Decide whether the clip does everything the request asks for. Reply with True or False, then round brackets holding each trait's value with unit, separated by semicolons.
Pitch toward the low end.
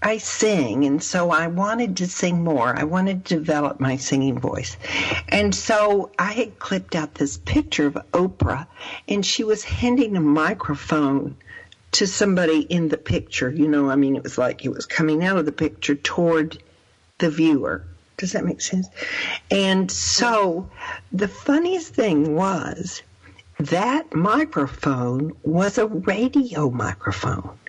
False (160 Hz)